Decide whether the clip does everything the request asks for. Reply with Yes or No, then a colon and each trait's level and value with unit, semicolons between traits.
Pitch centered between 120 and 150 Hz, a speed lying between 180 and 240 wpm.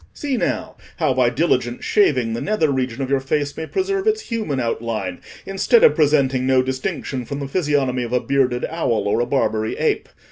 Yes: low, 135 Hz; average, 190 wpm